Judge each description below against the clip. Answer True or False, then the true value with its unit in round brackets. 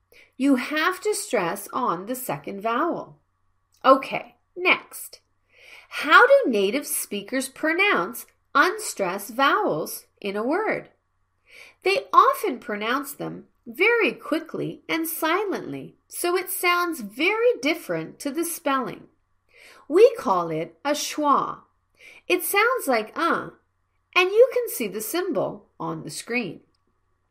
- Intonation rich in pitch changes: True (7.2 semitones)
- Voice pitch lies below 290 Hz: False (315 Hz)